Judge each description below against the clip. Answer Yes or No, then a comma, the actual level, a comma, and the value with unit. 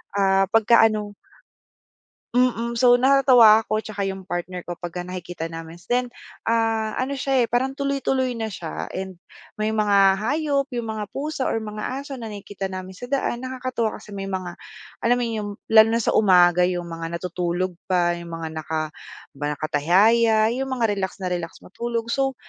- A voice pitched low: No, high, 215 Hz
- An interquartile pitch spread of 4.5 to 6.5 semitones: Yes, average, 5.0 semitones